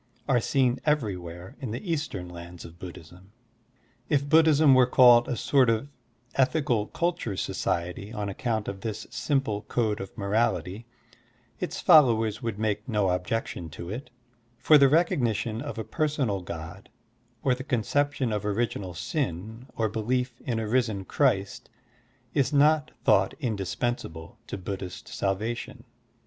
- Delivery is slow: No, average, 145 wpm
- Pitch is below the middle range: Yes, low, 115 Hz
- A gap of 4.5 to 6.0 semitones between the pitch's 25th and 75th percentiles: Yes, average, 5.2 semitones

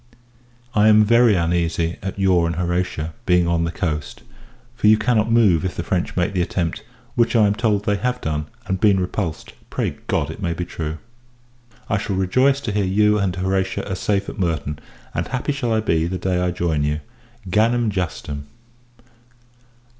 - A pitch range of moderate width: Yes, average, 3.9 semitones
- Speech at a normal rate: Yes, average, 185 wpm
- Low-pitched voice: Yes, very low, 95 Hz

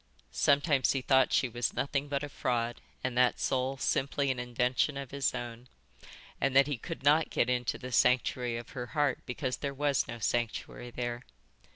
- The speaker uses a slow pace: No, average, 185 wpm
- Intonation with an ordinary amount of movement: No, narrow, 2.3 semitones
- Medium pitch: No, low, 130 Hz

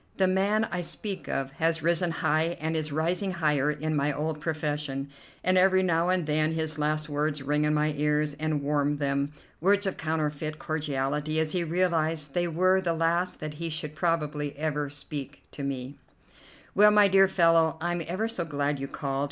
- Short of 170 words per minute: No, average, 185 wpm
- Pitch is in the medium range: Yes, medium, 155 Hz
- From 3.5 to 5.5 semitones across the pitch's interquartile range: No, narrow, 2.6 semitones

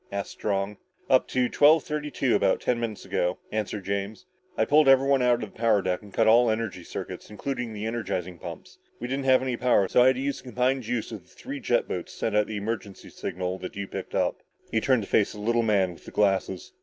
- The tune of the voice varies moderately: Yes, average, 4.1 semitones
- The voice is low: Yes, low, 110 Hz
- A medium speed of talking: No, fast, 245 wpm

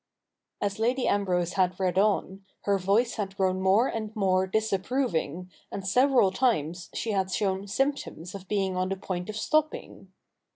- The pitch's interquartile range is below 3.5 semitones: Yes, average, 2.7 semitones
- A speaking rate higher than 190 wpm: No, average, 160 wpm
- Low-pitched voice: No, high, 195 Hz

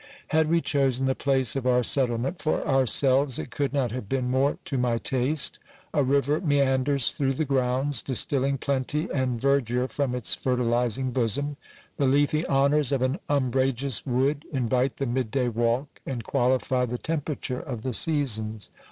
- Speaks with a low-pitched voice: Yes, low, 130 Hz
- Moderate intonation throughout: No, narrow, 2.2 semitones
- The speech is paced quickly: No, average, 170 wpm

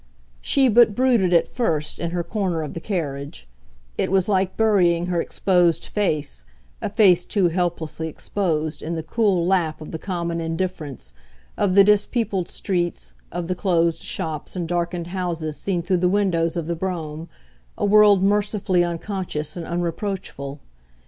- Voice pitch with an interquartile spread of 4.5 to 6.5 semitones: No, average, 2.9 semitones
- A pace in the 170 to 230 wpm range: No, average, 155 wpm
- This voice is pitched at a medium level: Yes, medium, 175 Hz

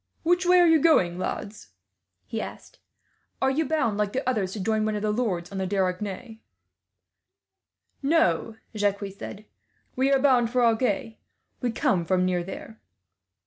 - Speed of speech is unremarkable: Yes, average, 160 wpm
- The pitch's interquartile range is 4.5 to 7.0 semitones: Yes, average, 5.1 semitones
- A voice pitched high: Yes, high, 220 Hz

